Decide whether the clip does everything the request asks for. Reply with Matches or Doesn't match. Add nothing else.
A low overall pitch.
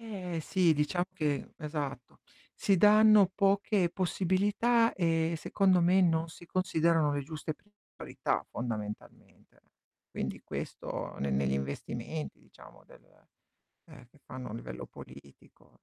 Doesn't match